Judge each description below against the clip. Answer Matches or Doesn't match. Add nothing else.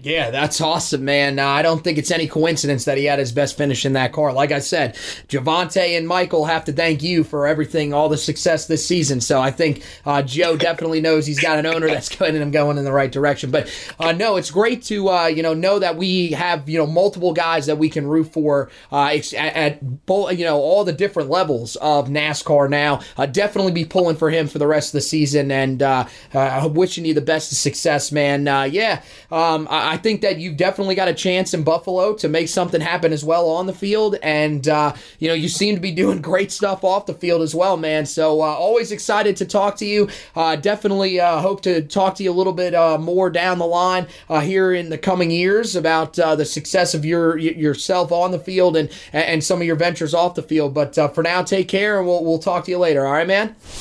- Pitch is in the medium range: Matches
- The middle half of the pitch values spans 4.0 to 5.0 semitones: Doesn't match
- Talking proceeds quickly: Matches